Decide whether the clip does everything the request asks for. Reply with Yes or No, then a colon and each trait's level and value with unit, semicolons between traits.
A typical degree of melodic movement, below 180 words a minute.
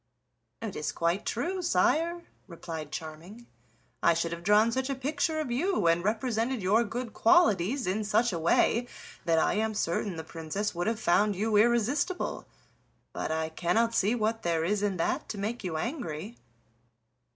No: wide, 5.9 semitones; average, 170 wpm